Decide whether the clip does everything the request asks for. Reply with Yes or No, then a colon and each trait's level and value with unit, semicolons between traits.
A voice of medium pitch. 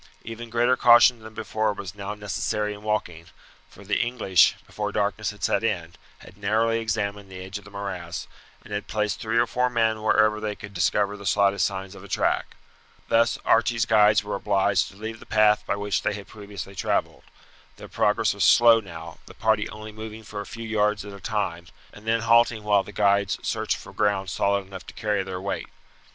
No: low, 105 Hz